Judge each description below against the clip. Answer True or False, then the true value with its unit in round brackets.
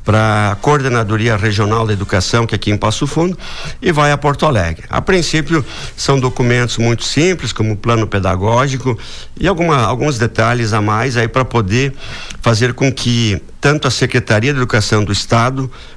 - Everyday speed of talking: True (175 wpm)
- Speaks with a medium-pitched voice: False (120 Hz)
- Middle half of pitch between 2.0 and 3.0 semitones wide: False (3.8 semitones)